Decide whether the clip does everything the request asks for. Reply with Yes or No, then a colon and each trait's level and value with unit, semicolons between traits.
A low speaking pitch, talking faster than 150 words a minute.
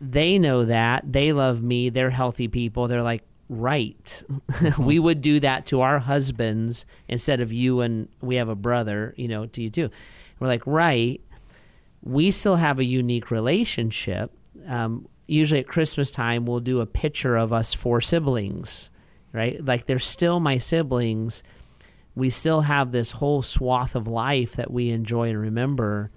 Yes: low, 125 Hz; average, 170 wpm